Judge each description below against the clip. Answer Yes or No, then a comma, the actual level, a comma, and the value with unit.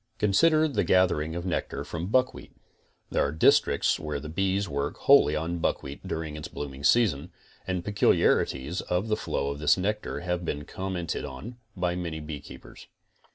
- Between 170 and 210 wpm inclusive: No, average, 160 wpm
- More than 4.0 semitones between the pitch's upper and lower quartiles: Yes, average, 4.5 semitones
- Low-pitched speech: Yes, very low, 85 Hz